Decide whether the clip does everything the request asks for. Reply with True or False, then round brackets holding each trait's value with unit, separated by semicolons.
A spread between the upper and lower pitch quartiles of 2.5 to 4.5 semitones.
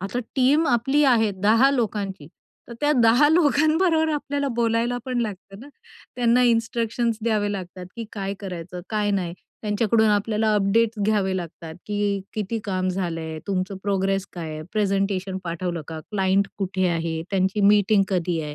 True (3.7 semitones)